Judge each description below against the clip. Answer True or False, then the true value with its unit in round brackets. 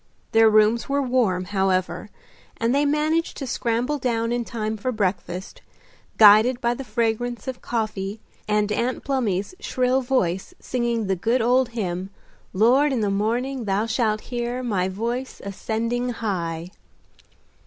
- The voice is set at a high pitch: True (230 Hz)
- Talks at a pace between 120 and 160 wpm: True (145 wpm)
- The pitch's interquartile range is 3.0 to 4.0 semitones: True (3.4 semitones)